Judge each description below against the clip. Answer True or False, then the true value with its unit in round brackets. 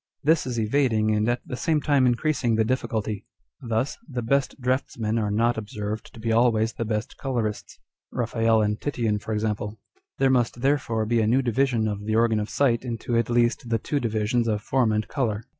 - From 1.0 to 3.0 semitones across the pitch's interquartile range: True (2.6 semitones)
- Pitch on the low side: True (115 Hz)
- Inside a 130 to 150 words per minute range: False (195 wpm)